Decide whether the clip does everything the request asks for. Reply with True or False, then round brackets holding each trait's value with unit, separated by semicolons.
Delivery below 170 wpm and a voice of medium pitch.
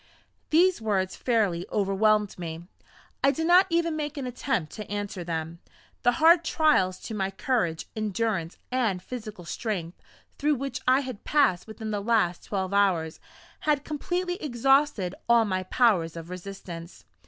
False (150 wpm; 215 Hz)